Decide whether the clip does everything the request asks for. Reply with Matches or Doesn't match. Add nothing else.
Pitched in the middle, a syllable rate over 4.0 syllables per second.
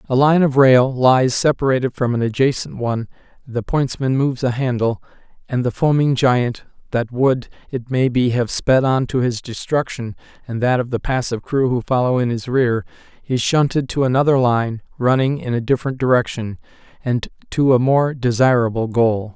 Doesn't match